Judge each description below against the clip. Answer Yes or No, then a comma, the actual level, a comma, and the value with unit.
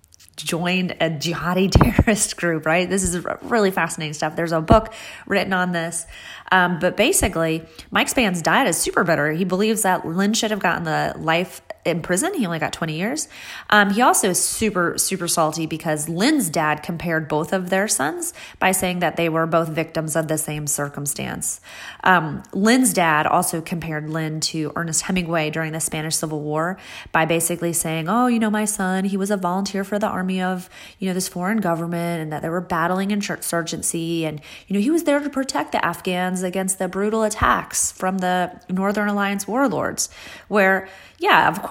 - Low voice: No, medium, 180 Hz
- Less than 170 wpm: No, average, 190 wpm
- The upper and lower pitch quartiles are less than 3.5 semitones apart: No, average, 3.8 semitones